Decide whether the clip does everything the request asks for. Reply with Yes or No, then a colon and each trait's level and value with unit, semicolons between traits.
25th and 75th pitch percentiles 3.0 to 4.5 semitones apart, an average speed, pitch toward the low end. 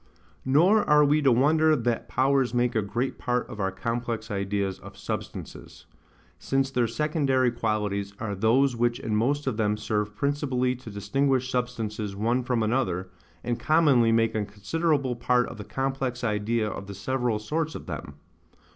Yes: average, 4.0 semitones; average, 165 wpm; low, 120 Hz